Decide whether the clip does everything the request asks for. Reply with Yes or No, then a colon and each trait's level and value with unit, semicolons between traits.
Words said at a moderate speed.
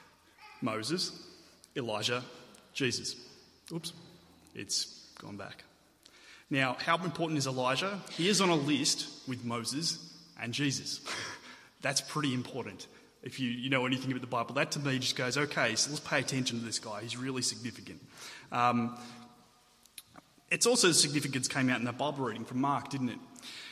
Yes: average, 160 wpm